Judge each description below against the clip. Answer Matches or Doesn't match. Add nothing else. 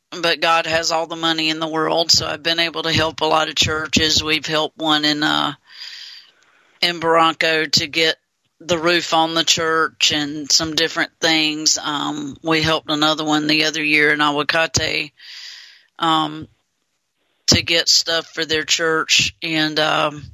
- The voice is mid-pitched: Matches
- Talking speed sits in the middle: Matches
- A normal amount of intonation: Doesn't match